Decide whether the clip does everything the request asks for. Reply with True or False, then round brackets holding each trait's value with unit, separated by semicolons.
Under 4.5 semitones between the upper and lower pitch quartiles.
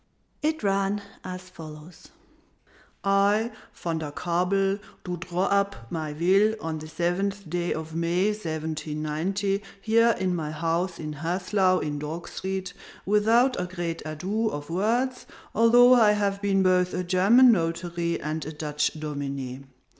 True (3.9 semitones)